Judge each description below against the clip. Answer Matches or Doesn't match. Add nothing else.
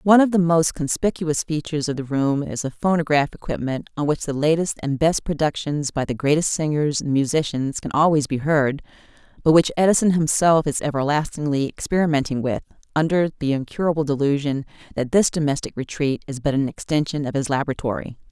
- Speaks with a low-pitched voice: Doesn't match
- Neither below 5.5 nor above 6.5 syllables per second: Matches